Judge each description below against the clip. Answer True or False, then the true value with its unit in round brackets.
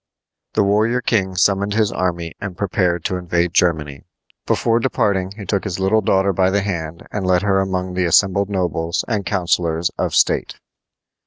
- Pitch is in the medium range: False (95 Hz)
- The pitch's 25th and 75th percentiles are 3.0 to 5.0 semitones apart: False (2.5 semitones)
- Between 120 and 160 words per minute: False (170 wpm)